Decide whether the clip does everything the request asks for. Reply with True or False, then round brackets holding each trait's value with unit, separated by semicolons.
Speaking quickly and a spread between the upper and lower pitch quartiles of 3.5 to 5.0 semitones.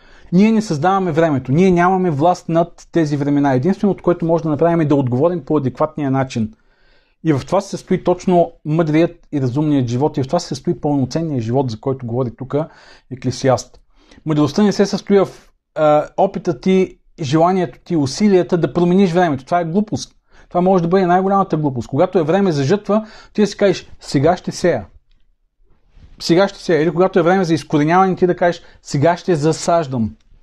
True (185 wpm; 3.9 semitones)